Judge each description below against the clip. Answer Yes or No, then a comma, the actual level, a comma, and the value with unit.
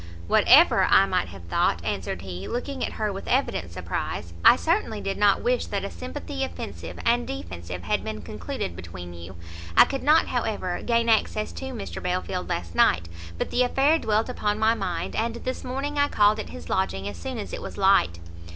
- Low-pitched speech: No, medium, 185 Hz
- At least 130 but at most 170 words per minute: No, average, 195 wpm